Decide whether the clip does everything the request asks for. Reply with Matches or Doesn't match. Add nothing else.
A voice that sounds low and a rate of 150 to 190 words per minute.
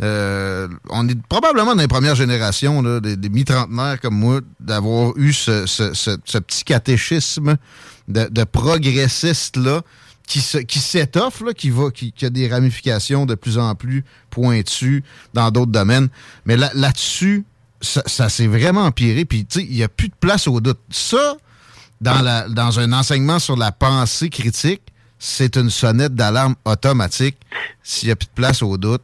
Matches